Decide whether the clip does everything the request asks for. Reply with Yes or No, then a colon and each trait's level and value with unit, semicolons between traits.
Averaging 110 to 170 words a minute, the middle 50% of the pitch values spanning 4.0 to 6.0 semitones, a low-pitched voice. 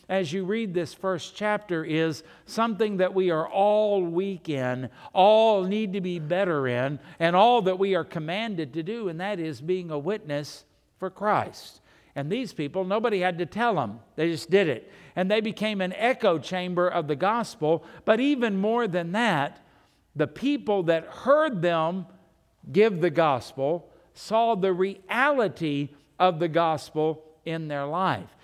No: average, 165 wpm; average, 4.4 semitones; medium, 180 Hz